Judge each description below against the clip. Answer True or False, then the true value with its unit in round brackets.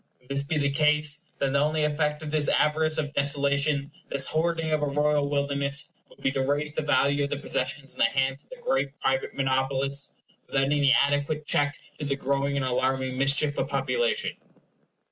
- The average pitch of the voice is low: False (145 Hz)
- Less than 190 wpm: False (195 wpm)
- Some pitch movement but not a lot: False (1.6 semitones)